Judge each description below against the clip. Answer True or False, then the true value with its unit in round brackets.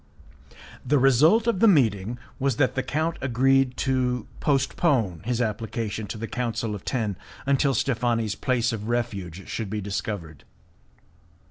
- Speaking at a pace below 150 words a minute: True (140 wpm)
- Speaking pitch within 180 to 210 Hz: False (120 Hz)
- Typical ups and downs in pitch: True (3.9 semitones)